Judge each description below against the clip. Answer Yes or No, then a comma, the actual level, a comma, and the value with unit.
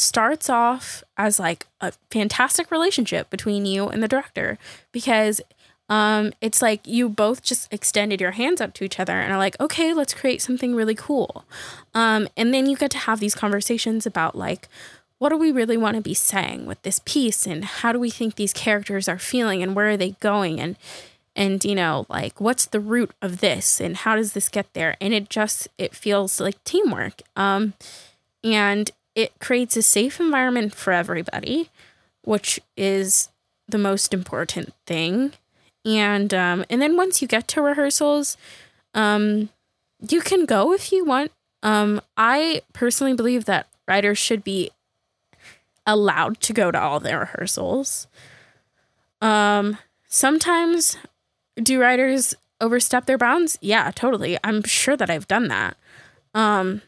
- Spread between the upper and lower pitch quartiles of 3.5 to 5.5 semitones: Yes, average, 4.2 semitones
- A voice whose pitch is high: Yes, high, 220 Hz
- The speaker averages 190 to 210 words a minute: No, average, 165 wpm